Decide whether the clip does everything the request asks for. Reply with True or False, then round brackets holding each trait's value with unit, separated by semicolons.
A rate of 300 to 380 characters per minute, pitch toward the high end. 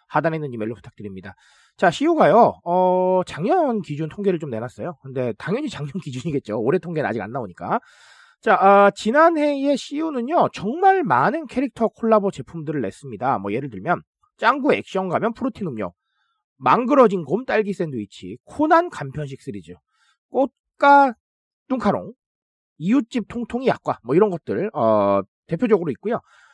True (330 characters per minute; 195 Hz)